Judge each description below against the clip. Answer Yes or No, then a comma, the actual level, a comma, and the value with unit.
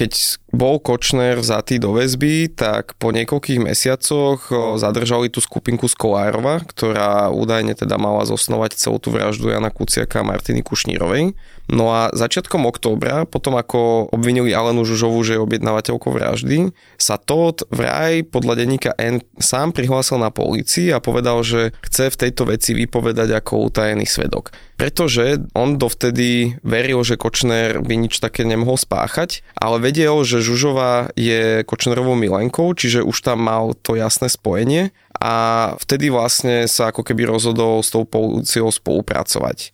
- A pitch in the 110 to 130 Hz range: Yes, low, 120 Hz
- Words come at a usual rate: Yes, average, 145 wpm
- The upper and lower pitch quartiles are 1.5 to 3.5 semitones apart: Yes, narrow, 2.4 semitones